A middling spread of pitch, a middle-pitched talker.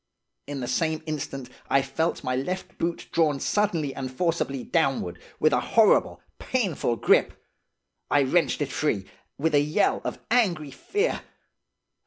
Yes: average, 4.0 semitones; medium, 155 Hz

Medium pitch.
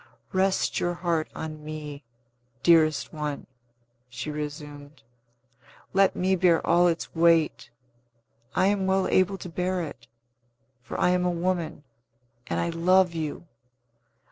Yes: medium, 170 Hz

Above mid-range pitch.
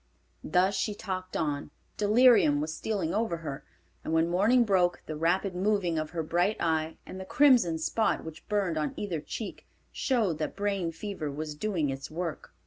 No: medium, 175 Hz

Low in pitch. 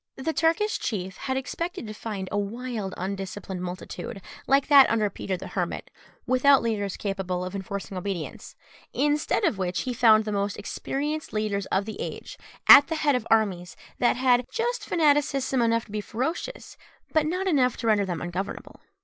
No: high, 225 Hz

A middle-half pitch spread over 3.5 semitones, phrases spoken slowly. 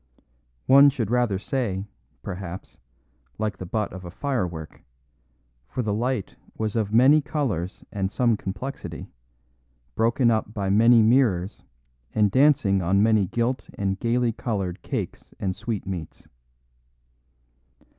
Yes: average, 4.1 semitones; slow, 125 wpm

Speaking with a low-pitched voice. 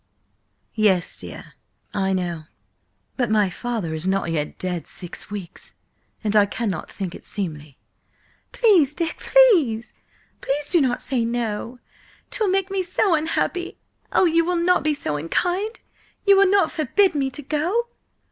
No: very high, 255 Hz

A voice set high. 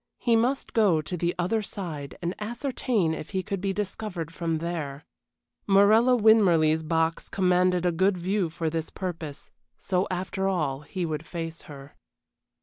No: medium, 180 Hz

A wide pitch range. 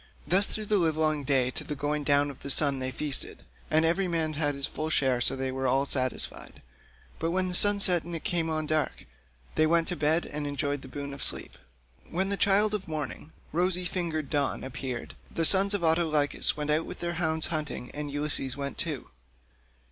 No: average, 3.3 semitones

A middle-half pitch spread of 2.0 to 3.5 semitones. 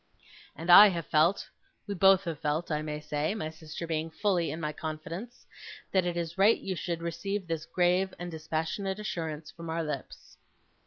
Yes: average, 3.2 semitones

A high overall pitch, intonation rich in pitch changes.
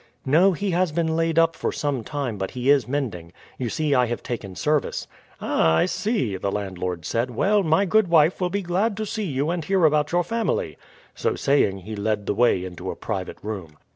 No: medium, 145 Hz; wide, 8.5 semitones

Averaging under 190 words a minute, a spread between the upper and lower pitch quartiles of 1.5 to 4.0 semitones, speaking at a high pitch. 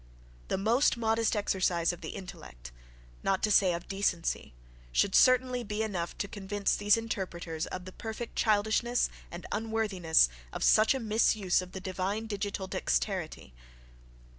Yes: average, 145 wpm; average, 3.5 semitones; high, 200 Hz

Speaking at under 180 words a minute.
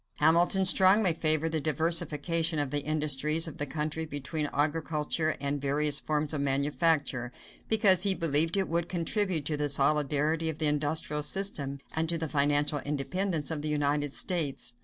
Yes: average, 160 wpm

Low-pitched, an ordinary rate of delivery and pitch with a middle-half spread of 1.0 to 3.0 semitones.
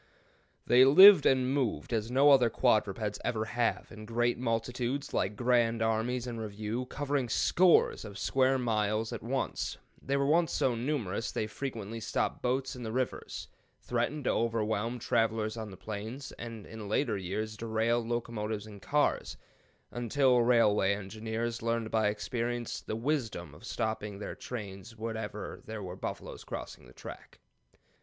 Yes: low, 115 Hz; average, 150 wpm; narrow, 2.6 semitones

